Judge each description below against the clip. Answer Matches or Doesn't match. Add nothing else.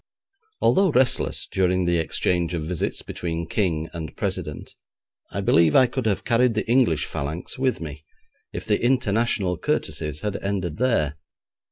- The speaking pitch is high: Doesn't match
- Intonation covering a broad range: Matches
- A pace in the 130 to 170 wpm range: Matches